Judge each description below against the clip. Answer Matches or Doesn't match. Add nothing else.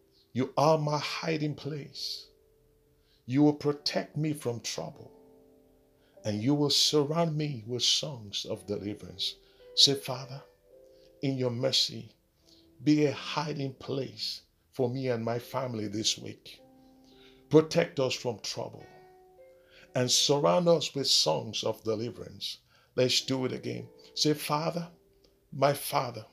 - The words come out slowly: Matches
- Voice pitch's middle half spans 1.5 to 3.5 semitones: Doesn't match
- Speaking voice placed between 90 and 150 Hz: Matches